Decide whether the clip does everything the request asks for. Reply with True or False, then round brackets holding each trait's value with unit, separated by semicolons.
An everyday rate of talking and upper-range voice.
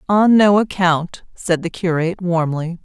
False (150 wpm; 175 Hz)